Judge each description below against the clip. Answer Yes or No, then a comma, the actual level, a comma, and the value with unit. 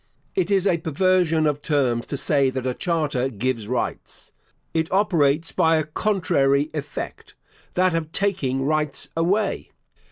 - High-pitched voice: No, medium, 155 Hz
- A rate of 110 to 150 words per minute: Yes, average, 140 wpm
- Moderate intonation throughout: Yes, average, 4.2 semitones